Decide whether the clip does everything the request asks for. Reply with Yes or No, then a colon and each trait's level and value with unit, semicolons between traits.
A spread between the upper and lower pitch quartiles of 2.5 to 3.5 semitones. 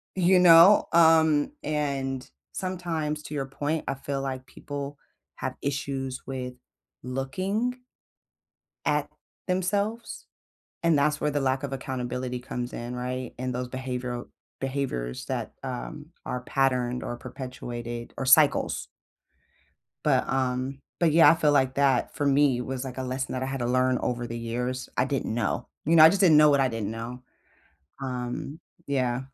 Yes: average, 3.0 semitones